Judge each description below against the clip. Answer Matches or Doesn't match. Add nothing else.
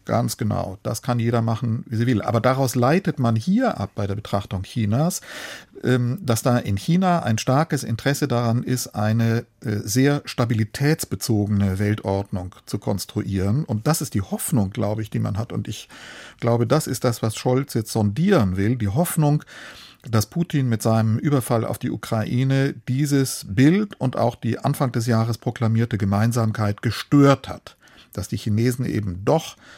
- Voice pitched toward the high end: Doesn't match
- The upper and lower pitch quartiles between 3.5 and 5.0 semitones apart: Matches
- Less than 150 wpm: Doesn't match